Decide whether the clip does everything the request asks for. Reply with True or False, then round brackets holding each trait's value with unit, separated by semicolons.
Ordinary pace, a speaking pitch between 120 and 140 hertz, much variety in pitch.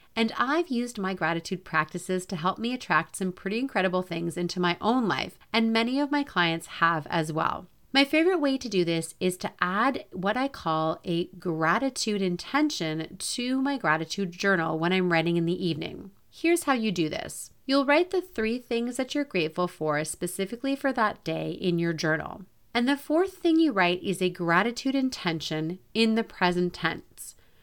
False (185 wpm; 190 Hz; 6.9 semitones)